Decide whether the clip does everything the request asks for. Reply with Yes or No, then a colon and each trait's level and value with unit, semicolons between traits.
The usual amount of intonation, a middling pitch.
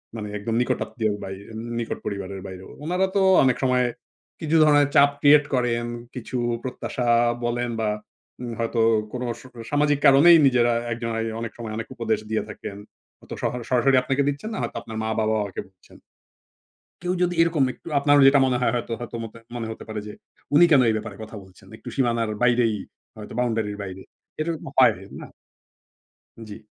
No: average, 3.8 semitones; low, 120 Hz